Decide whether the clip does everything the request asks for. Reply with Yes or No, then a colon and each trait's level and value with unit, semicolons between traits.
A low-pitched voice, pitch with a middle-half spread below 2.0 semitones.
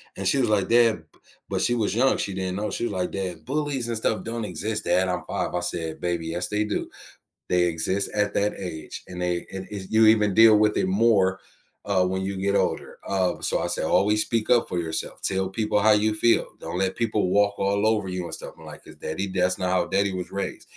No: low, 100 Hz; average, 2.8 semitones